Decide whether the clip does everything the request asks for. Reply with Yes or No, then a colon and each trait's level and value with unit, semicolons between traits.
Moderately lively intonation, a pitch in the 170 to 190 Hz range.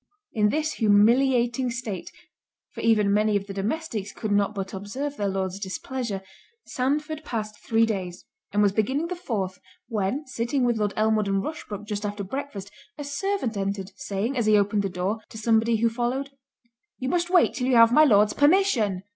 No: average, 4.5 semitones; high, 220 Hz